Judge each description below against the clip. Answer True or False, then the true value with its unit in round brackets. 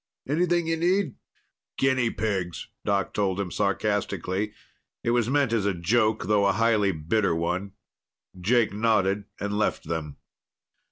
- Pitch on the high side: False (105 Hz)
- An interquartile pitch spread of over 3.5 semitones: True (4.0 semitones)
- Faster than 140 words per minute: False (135 wpm)